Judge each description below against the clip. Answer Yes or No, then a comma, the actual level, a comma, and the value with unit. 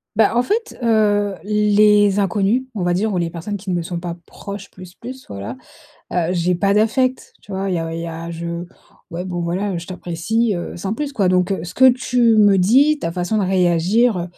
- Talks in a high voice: Yes, high, 195 Hz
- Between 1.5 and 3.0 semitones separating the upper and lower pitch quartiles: No, average, 3.7 semitones